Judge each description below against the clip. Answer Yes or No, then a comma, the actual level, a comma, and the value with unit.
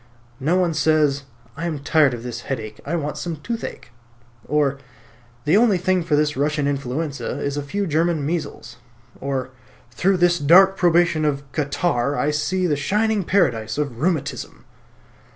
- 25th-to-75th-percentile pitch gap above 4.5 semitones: No, average, 3.9 semitones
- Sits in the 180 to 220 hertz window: No, medium, 150 Hz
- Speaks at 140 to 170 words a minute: Yes, average, 155 wpm